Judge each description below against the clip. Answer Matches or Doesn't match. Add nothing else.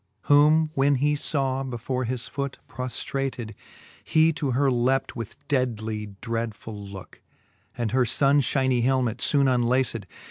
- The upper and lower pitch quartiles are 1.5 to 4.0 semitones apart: Matches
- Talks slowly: Matches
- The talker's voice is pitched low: Matches